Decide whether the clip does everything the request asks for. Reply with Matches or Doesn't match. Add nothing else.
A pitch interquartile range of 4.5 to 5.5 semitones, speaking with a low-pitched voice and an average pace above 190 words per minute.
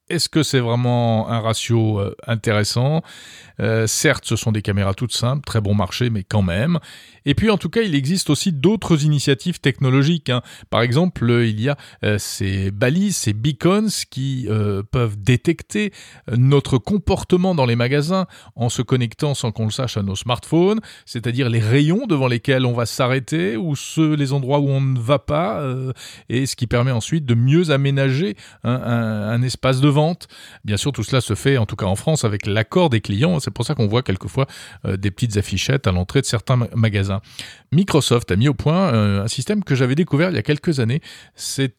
Matches